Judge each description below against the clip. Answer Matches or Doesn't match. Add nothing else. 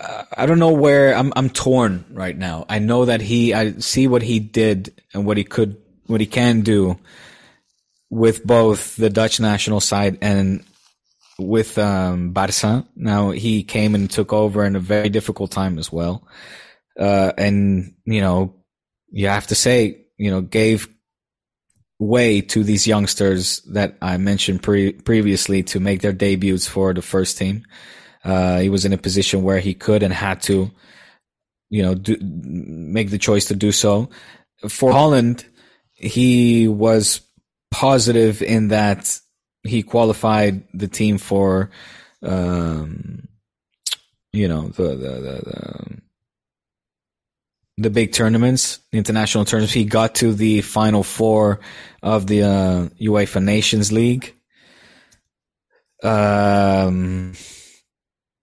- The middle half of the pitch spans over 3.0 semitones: Doesn't match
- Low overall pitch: Matches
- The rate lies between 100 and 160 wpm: Matches